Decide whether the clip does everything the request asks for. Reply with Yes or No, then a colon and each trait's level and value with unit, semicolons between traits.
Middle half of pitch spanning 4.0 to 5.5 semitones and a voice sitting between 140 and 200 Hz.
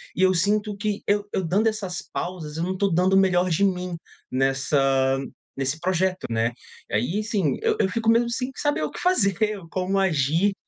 Yes: average, 4.6 semitones; medium, 185 Hz